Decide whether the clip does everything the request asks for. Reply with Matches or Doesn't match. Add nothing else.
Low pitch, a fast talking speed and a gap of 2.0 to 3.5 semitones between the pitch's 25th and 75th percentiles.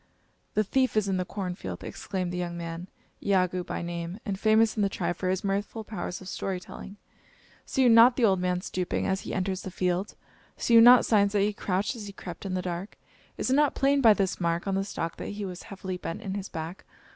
Doesn't match